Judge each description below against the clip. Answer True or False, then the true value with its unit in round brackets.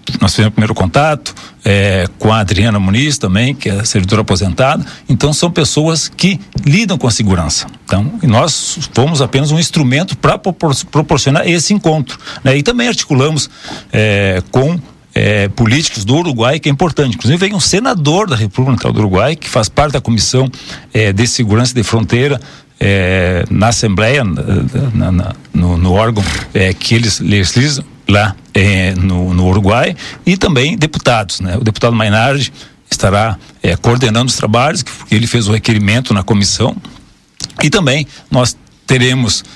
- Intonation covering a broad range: True (5.7 semitones)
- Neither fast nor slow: True (160 wpm)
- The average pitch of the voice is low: True (120 Hz)